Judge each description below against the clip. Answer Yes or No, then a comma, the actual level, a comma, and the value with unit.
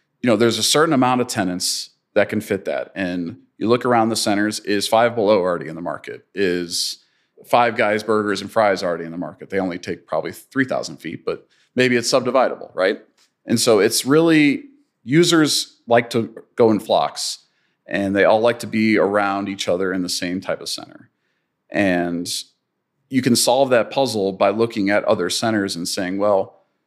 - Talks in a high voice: No, low, 110 Hz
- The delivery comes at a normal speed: Yes, average, 190 wpm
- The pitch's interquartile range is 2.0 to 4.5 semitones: Yes, average, 3.8 semitones